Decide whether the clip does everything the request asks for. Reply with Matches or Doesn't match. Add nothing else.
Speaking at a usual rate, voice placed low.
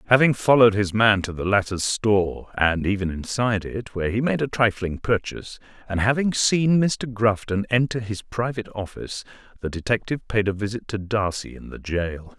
Matches